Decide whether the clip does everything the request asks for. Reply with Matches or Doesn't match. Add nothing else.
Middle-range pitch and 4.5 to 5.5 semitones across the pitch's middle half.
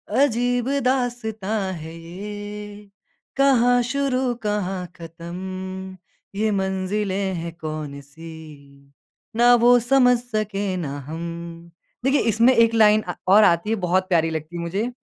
Doesn't match